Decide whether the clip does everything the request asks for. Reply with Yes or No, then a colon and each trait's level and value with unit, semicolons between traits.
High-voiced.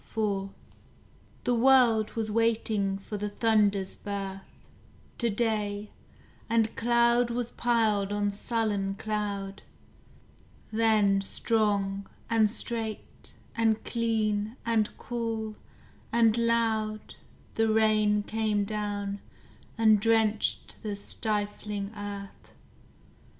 Yes: high, 215 Hz